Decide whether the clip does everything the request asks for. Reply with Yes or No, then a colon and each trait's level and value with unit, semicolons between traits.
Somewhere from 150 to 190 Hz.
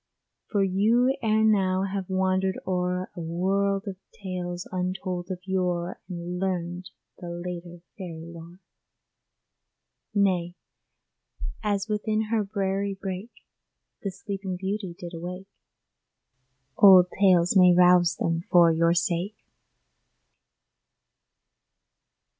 Yes: medium, 185 Hz